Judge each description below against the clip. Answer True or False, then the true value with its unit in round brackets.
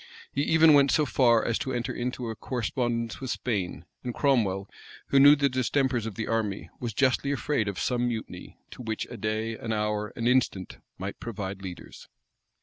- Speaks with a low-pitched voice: True (120 Hz)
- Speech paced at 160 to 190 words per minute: True (185 wpm)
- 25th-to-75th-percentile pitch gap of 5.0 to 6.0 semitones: False (3.4 semitones)